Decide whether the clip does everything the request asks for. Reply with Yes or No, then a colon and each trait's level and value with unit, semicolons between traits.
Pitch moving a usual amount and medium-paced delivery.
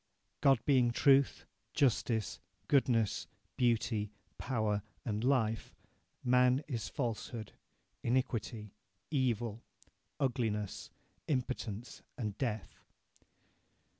No: average, 3.2 semitones; slow, 75 wpm